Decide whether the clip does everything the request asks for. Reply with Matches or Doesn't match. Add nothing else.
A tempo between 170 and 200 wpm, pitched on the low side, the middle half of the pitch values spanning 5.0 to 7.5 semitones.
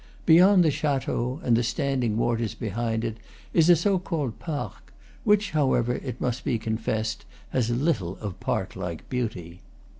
Doesn't match